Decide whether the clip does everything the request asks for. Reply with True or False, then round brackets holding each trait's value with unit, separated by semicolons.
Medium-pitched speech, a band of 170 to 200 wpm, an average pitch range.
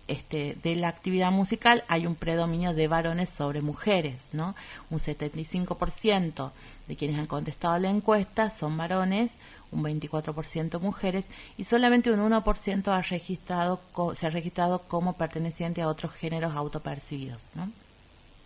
False (170 Hz; 140 wpm; 3.1 semitones)